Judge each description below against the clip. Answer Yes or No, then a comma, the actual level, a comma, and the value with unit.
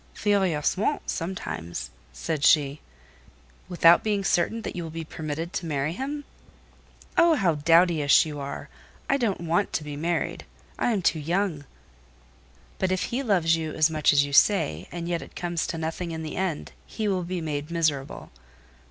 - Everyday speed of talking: Yes, average, 170 wpm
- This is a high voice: No, medium, 165 Hz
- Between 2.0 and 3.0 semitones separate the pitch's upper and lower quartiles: No, average, 3.5 semitones